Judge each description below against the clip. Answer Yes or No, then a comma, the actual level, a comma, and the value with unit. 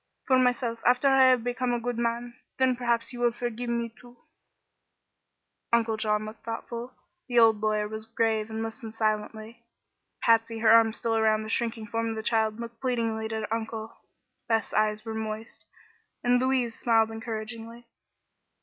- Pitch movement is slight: Yes, narrow, 1.5 semitones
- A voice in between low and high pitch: No, high, 230 Hz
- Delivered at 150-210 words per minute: Yes, average, 165 wpm